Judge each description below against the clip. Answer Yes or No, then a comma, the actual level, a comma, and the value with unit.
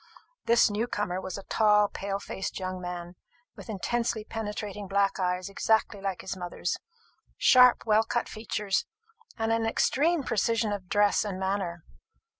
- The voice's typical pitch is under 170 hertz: No, high, 205 Hz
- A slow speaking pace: No, average, 150 wpm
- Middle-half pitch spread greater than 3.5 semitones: No, average, 2.8 semitones